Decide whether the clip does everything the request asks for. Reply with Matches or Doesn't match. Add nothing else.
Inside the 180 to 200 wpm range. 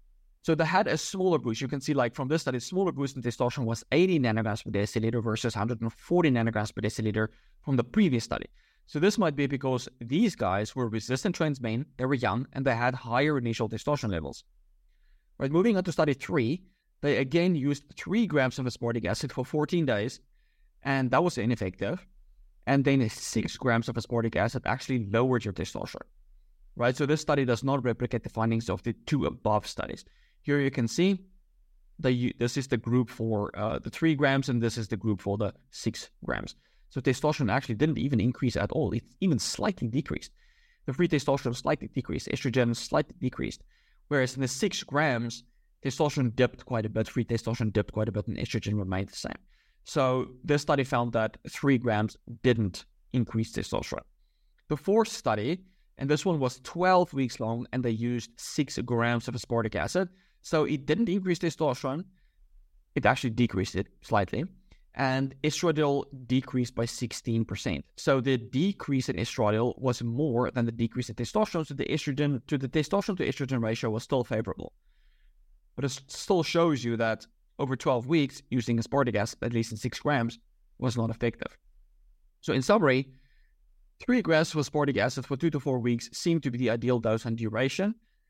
Matches